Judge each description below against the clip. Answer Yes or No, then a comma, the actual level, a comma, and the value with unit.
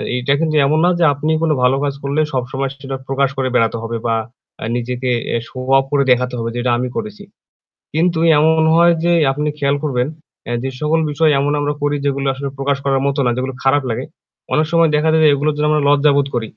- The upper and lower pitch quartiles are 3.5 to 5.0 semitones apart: No, average, 2.8 semitones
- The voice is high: No, medium, 140 Hz